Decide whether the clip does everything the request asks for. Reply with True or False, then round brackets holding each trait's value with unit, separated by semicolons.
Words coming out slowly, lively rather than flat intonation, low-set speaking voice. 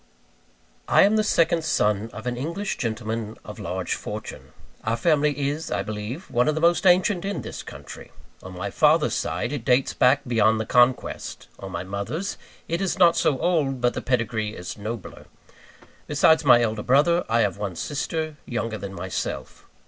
False (180 wpm; 6.5 semitones; 125 Hz)